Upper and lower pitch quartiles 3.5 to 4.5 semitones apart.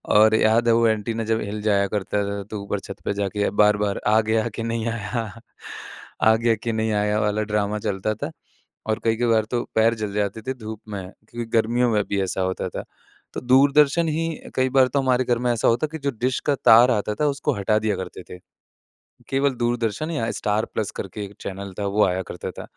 No: narrow, 2.5 semitones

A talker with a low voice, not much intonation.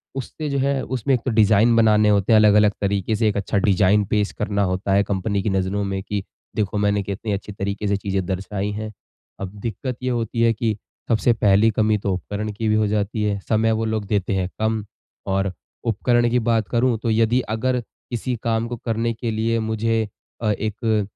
Yes: low, 105 Hz; narrow, 2.1 semitones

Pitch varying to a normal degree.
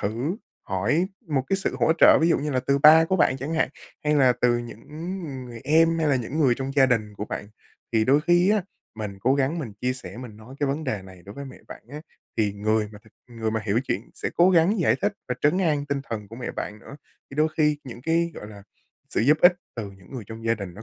No: wide, 6.0 semitones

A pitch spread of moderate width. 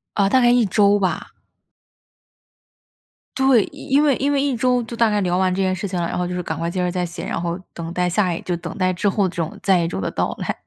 Yes: average, 4.7 semitones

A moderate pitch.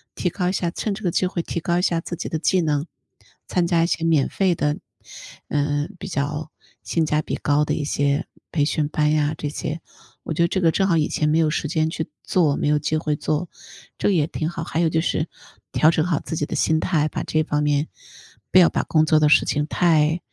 Yes: medium, 155 Hz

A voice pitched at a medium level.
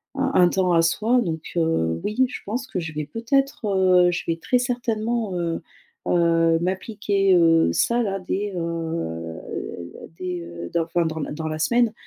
Yes: medium, 180 Hz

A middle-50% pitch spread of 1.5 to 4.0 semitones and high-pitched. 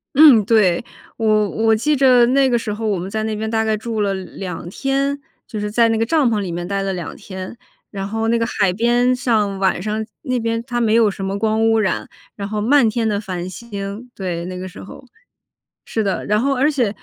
Yes: average, 3.1 semitones; high, 220 Hz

